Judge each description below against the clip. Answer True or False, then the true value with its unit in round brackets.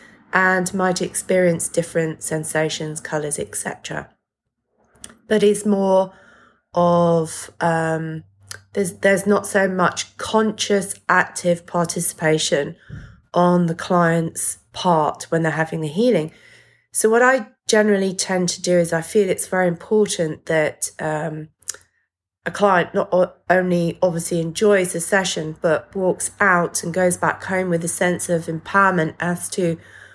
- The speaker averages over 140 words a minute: False (135 wpm)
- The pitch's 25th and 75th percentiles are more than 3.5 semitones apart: False (3.0 semitones)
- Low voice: False (175 Hz)